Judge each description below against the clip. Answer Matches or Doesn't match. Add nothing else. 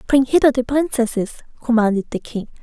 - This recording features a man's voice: Doesn't match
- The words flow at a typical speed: Matches